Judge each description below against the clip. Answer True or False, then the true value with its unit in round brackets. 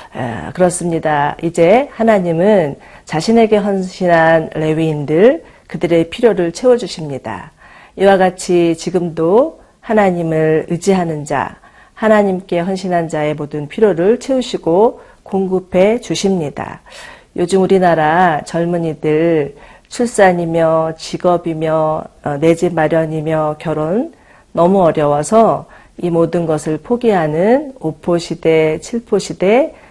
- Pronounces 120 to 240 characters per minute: False (255 characters per minute)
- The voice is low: False (175 Hz)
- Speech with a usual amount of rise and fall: True (3.6 semitones)